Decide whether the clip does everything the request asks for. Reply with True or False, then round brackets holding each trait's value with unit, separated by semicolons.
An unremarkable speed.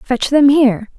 True (185 wpm)